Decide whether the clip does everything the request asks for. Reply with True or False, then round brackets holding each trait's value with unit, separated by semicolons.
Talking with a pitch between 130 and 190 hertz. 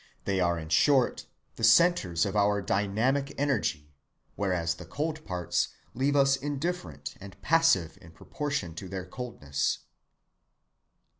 False (100 Hz)